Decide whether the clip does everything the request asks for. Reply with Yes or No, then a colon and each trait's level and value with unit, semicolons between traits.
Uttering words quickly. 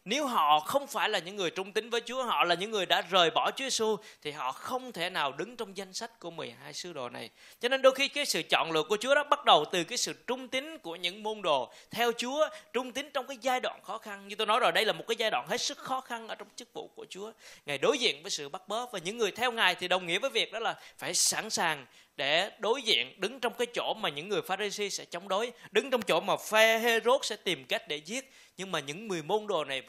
Yes: fast, 280 wpm